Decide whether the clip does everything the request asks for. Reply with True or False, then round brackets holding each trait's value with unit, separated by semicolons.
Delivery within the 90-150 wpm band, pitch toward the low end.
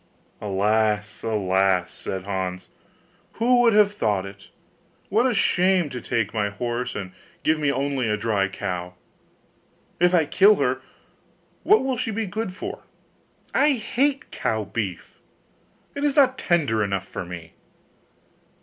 True (140 wpm; 115 Hz)